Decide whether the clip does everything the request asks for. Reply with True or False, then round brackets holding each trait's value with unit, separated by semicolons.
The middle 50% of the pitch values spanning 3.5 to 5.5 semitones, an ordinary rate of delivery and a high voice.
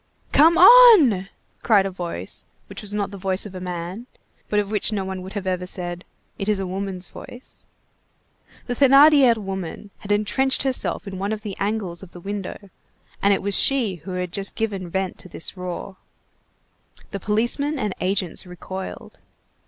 False (2.8 semitones; 175 wpm; 195 Hz)